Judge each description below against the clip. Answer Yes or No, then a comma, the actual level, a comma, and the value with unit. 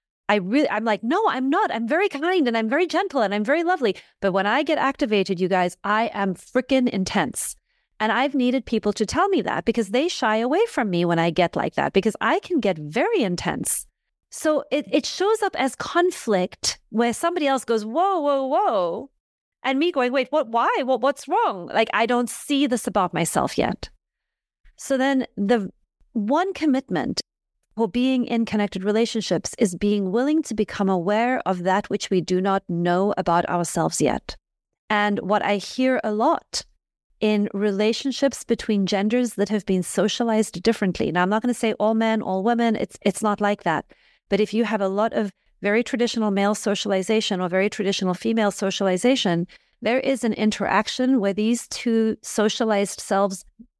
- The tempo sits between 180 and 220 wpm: Yes, average, 185 wpm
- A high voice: Yes, high, 220 Hz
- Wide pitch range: No, average, 4.7 semitones